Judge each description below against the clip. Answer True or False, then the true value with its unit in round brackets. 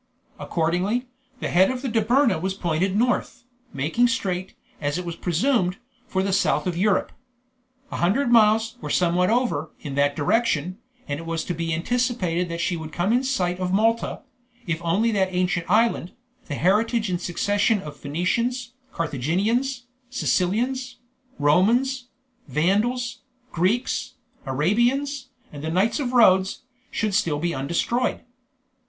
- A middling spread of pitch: False (5.9 semitones)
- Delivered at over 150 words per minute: False (140 wpm)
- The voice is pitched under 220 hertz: True (190 Hz)